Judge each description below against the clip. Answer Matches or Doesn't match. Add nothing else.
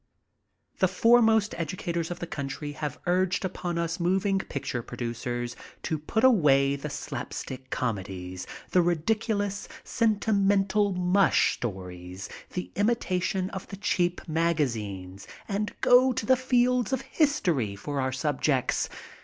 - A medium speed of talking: Doesn't match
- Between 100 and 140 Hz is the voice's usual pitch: Doesn't match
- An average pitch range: Doesn't match